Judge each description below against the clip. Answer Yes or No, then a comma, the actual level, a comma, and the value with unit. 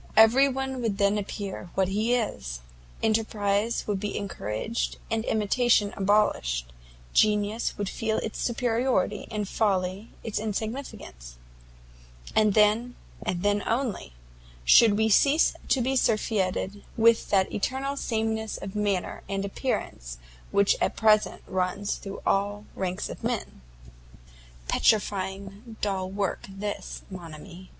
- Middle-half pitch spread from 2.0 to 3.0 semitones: Yes, narrow, 2.5 semitones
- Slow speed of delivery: Yes, slow, 125 wpm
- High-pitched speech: Yes, high, 205 Hz